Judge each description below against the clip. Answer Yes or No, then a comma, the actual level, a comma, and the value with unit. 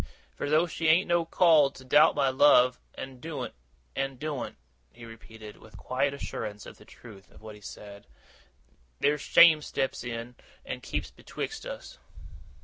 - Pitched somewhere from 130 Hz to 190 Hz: Yes, low, 135 Hz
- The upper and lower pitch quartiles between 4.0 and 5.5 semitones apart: Yes, average, 5.1 semitones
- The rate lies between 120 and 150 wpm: No, average, 165 wpm